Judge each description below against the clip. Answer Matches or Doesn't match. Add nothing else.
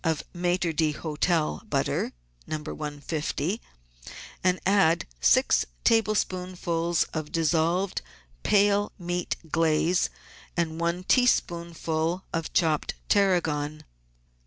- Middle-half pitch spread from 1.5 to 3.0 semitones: Matches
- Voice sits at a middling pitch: Matches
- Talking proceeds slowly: Matches